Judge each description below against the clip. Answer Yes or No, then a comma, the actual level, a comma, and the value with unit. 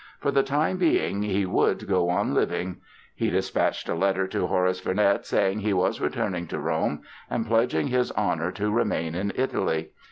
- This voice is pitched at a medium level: No, low, 100 Hz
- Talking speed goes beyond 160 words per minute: Yes, average, 180 wpm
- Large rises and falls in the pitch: No, average, 3.9 semitones